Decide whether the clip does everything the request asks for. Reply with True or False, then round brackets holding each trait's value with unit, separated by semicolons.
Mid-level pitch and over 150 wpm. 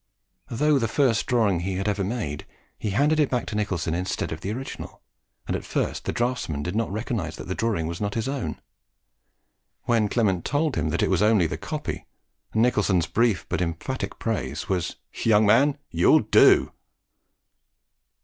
False (105 Hz; 175 wpm)